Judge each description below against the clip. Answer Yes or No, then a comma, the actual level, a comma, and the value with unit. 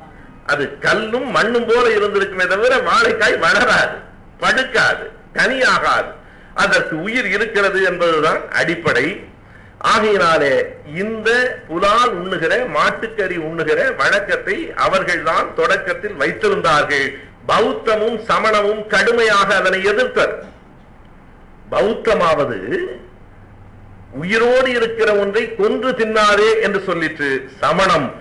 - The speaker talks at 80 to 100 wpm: Yes, average, 85 wpm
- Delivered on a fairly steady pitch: No, average, 5.1 semitones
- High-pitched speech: Yes, high, 220 Hz